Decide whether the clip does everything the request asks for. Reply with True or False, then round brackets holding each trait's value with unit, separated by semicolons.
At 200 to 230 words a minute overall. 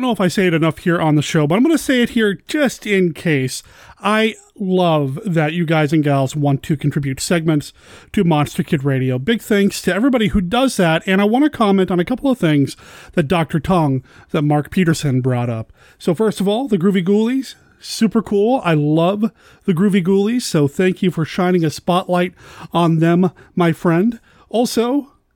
True (205 wpm)